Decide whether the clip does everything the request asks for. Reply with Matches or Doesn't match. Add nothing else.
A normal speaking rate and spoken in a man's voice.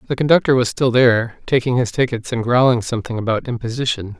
Matches